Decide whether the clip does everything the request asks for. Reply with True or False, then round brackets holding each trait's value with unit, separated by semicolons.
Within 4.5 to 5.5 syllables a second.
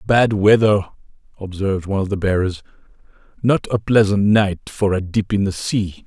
True (5.2 syllables/s)